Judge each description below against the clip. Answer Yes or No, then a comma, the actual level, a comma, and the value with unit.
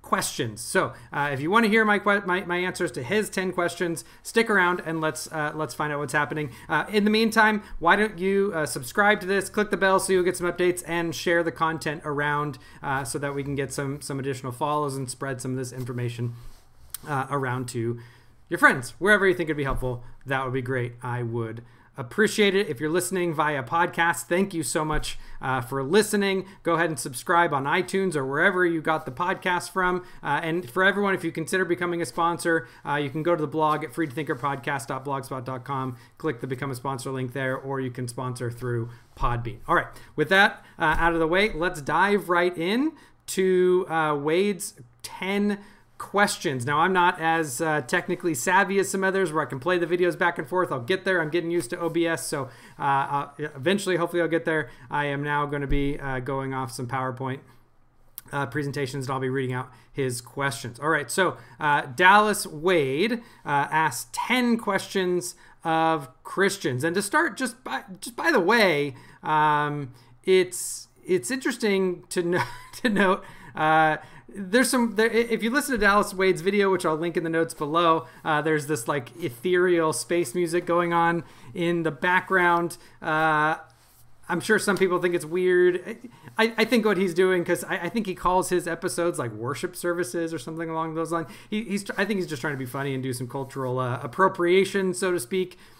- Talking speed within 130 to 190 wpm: No, average, 200 wpm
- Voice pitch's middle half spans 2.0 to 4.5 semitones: No, average, 4.9 semitones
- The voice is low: No, medium, 165 Hz